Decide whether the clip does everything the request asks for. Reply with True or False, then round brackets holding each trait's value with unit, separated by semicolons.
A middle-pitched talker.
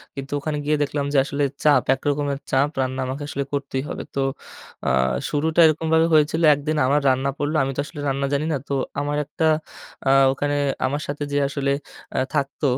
True (145 Hz)